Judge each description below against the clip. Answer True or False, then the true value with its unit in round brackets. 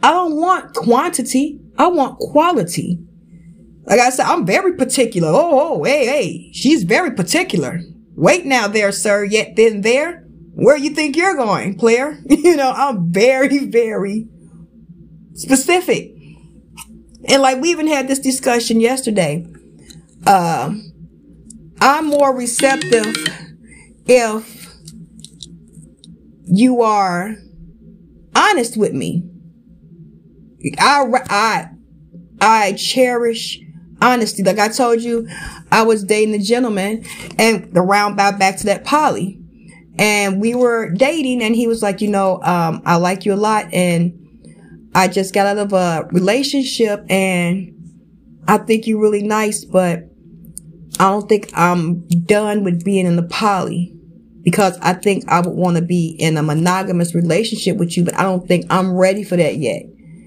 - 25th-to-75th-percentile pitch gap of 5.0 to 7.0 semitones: True (5.3 semitones)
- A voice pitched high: True (205 Hz)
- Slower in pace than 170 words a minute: True (140 wpm)